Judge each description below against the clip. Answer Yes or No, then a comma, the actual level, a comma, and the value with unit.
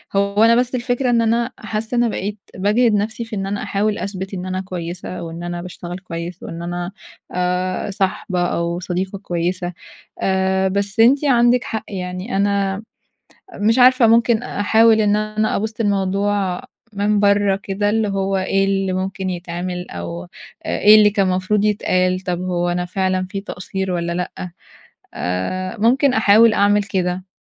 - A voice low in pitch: No, high, 195 Hz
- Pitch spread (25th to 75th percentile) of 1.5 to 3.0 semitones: Yes, average, 2.7 semitones